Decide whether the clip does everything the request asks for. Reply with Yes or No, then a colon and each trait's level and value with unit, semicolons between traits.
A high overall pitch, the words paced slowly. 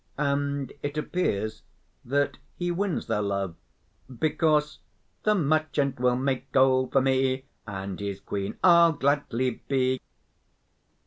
No: low, 135 Hz; slow, 120 wpm